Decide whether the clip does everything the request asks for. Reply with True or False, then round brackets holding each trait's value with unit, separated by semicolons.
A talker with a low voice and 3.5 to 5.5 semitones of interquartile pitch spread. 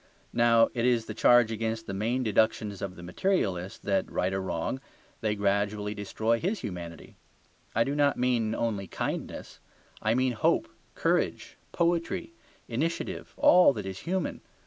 True (110 Hz; 3.9 semitones)